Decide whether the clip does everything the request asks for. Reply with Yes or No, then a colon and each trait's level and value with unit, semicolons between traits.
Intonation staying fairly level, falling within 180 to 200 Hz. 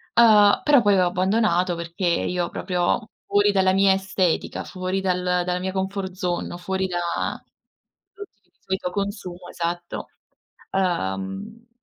Yes: narrow, 2.0 semitones; medium, 185 Hz